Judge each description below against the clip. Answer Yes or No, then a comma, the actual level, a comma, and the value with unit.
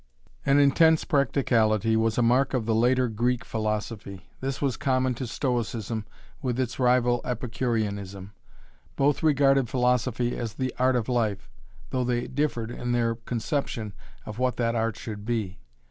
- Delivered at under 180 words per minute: Yes, average, 150 wpm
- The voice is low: Yes, low, 120 Hz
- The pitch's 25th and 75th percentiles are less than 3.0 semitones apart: Yes, narrow, 2.5 semitones